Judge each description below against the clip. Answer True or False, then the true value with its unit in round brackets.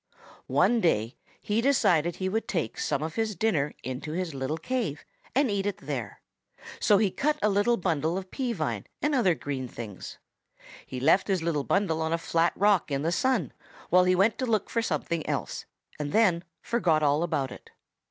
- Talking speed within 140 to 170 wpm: False (190 wpm)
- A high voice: False (175 Hz)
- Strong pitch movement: True (5.9 semitones)